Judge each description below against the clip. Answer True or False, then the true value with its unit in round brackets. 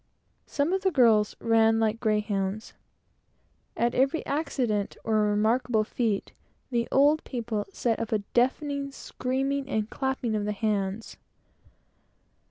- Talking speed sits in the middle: False (120 wpm)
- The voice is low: False (230 Hz)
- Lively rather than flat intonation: False (3.9 semitones)